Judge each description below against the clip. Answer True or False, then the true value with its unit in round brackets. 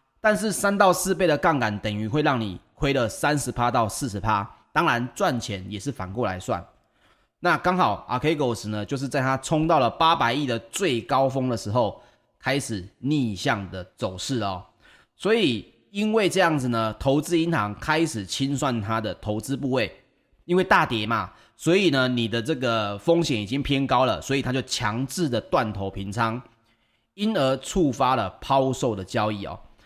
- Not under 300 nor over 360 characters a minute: False (265 characters per minute)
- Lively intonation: False (5.0 semitones)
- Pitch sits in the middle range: False (130 Hz)